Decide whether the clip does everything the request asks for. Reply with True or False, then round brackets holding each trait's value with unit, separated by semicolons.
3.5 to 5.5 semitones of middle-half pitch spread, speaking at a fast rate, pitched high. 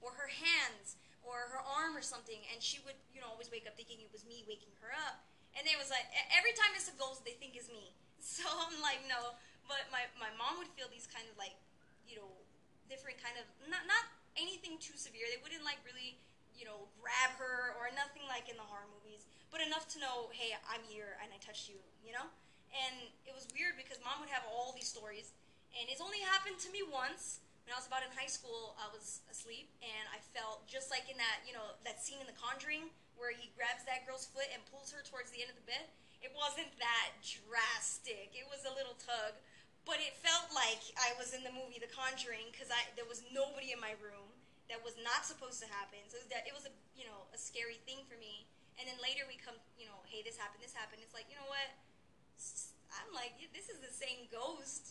False (3.1 semitones; 235 wpm; 250 Hz)